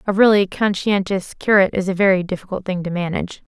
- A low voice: No, high, 190 Hz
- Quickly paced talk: No, average, 190 wpm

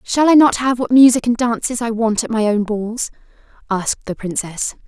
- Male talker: No, female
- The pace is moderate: No, fast, 210 wpm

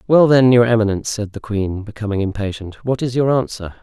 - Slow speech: No, fast, 205 wpm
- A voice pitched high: No, low, 110 Hz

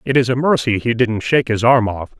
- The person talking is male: Yes, male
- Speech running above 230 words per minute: Yes, fast, 275 wpm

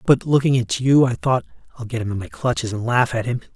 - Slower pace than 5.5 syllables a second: No, 6.1 syllables/s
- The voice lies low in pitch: Yes, low, 120 Hz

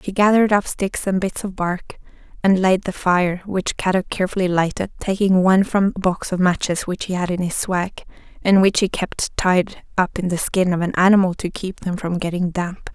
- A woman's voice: Yes, female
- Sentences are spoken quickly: Yes, fast, 220 wpm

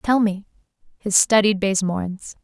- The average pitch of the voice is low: No, high, 200 Hz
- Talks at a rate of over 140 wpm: No, slow, 125 wpm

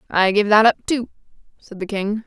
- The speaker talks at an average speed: No, fast, 210 wpm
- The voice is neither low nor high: No, high, 210 Hz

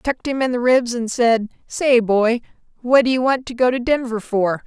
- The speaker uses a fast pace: Yes, fast, 230 wpm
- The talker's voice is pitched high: Yes, high, 240 Hz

